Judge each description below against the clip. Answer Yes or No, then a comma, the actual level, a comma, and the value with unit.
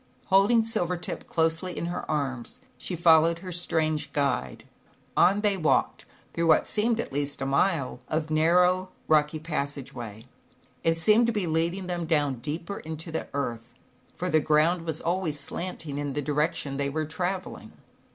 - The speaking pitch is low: No, medium, 160 Hz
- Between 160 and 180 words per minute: Yes, average, 165 wpm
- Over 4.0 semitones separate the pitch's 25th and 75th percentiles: No, average, 3.6 semitones